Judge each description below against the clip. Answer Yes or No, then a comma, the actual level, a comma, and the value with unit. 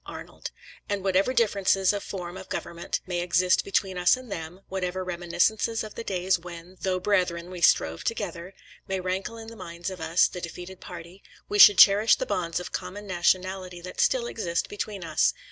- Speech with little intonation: Yes, narrow, 2.3 semitones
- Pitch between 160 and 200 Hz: Yes, medium, 185 Hz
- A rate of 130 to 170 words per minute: No, average, 185 wpm